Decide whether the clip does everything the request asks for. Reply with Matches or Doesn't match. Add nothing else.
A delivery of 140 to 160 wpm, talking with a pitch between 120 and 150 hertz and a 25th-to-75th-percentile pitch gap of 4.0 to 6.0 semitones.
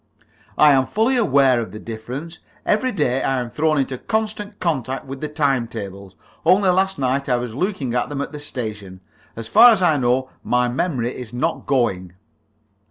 Doesn't match